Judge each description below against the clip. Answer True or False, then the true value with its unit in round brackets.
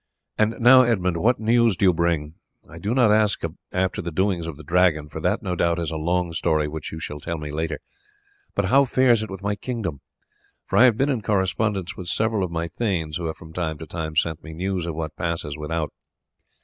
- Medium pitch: False (90 Hz)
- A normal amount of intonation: True (4.8 semitones)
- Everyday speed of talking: False (225 wpm)